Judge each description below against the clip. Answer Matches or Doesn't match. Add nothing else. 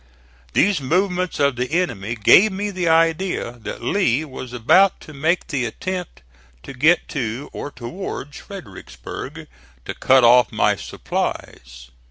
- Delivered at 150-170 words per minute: Doesn't match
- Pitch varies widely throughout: Matches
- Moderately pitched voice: Matches